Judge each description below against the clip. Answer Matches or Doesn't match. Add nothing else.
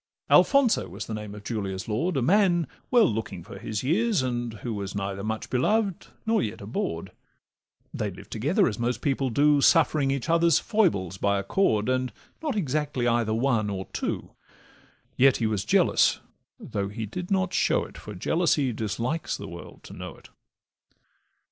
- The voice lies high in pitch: Doesn't match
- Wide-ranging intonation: Matches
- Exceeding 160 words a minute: Matches